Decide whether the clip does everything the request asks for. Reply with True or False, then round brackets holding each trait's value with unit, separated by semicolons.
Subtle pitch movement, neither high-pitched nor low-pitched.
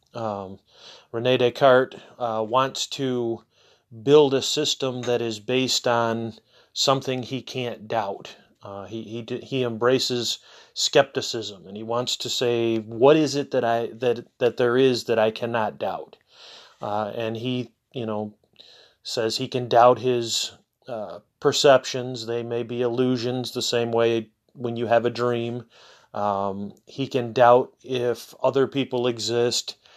False (1.9 semitones; 120 Hz)